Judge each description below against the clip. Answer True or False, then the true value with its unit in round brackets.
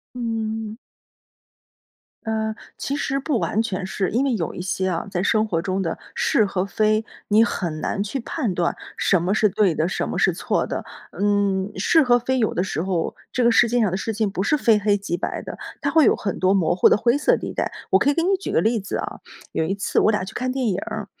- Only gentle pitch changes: False (3.7 semitones)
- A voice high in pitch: True (210 Hz)